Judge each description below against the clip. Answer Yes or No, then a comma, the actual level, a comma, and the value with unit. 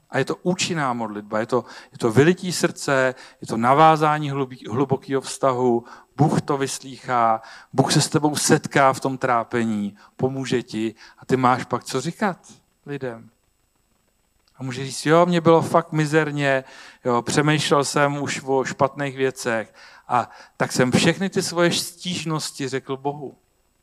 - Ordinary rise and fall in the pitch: Yes, average, 4.0 semitones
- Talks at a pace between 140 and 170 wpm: Yes, average, 150 wpm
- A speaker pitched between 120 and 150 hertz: Yes, low, 135 Hz